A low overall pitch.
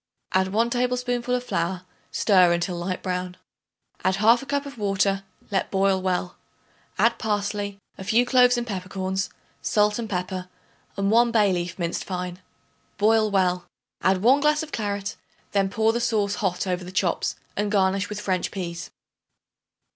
No: high, 200 Hz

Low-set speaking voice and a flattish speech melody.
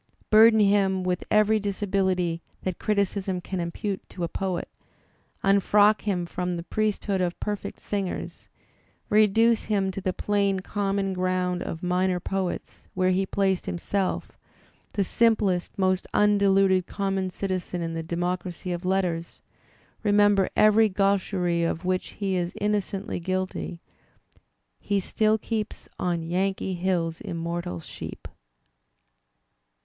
No: high, 190 Hz; narrow, 2.2 semitones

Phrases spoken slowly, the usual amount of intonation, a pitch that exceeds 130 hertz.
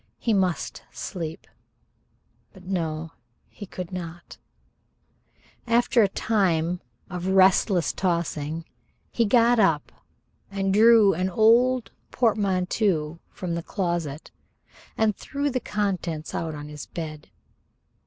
Yes: slow, 110 wpm; average, 4.4 semitones; medium, 185 Hz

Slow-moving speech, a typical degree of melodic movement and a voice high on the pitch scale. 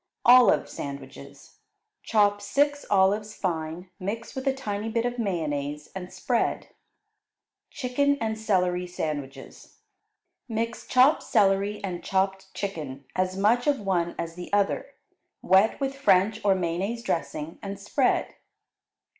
Yes: slow, 125 wpm; average, 4.6 semitones; high, 195 Hz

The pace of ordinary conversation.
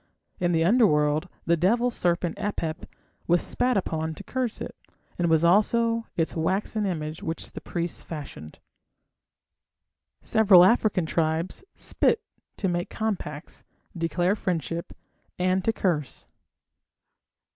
No: slow, 120 wpm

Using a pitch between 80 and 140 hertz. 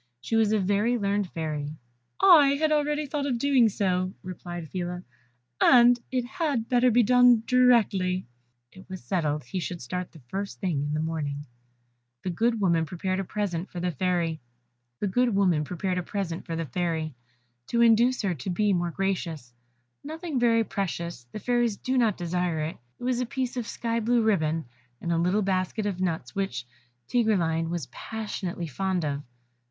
No: high, 190 Hz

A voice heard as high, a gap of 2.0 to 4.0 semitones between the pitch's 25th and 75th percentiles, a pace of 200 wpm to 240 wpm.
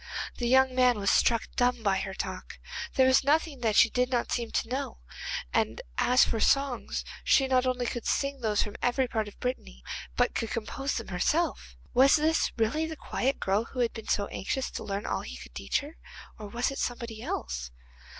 Yes: high, 245 Hz; average, 3.5 semitones; fast, 205 wpm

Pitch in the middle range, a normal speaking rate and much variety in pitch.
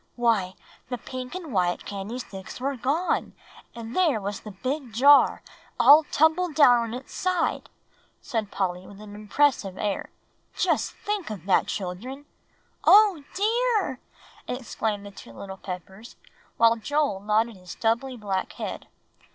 No: high, 230 Hz; average, 145 wpm; wide, 6.2 semitones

